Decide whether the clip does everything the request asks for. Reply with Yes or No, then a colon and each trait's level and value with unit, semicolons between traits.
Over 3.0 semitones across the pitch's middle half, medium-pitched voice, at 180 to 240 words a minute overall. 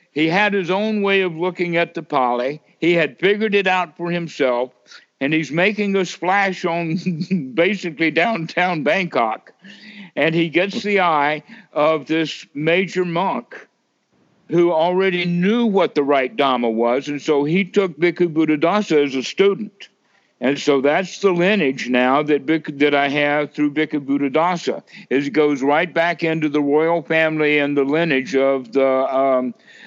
No: average, 4.0 semitones; medium, 160 Hz; average, 160 wpm